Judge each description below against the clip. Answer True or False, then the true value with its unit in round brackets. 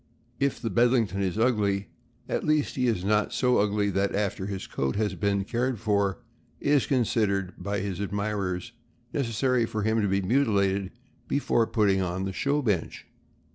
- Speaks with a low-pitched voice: True (105 Hz)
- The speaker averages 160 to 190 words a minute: True (170 wpm)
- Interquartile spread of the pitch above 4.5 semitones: False (3.4 semitones)